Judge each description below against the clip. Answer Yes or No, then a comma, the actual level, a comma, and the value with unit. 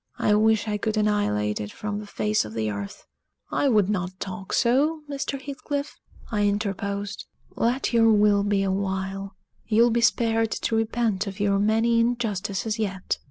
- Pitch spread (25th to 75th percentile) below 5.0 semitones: Yes, average, 2.8 semitones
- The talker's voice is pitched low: No, high, 210 Hz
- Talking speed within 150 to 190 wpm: Yes, average, 165 wpm